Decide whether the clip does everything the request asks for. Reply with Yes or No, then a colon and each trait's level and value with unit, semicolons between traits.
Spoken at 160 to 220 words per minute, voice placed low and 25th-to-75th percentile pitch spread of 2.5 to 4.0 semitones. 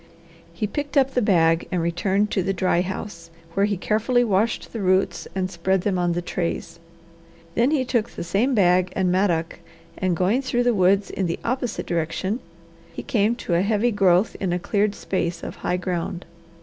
No: average, 190 wpm; high, 190 Hz; average, 3.6 semitones